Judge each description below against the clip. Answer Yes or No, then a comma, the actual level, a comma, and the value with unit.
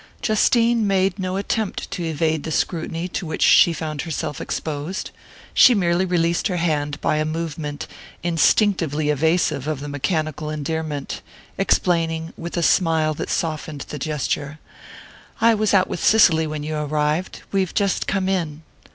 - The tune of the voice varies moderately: Yes, average, 3.3 semitones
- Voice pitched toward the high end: No, medium, 160 Hz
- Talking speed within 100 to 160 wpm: Yes, average, 150 wpm